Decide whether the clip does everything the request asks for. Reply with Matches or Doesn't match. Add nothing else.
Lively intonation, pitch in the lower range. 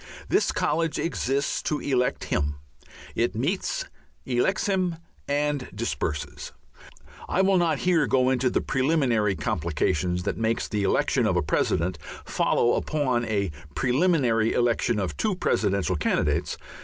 Matches